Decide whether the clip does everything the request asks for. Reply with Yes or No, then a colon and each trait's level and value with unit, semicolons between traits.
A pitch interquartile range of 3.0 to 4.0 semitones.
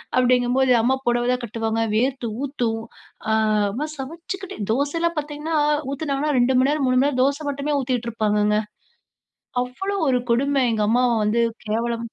Yes: average, 3.3 semitones